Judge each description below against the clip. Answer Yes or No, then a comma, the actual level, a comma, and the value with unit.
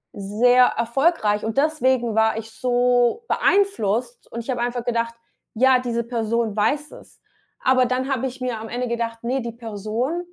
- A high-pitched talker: Yes, high, 240 Hz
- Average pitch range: No, narrow, 2.1 semitones